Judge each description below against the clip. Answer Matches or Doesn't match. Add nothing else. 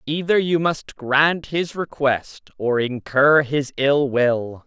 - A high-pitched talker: Doesn't match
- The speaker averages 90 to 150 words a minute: Matches